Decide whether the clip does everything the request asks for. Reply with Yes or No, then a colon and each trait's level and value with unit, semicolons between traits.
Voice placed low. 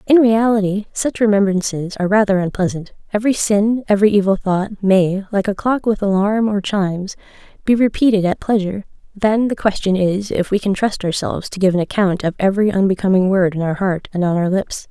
No: high, 200 Hz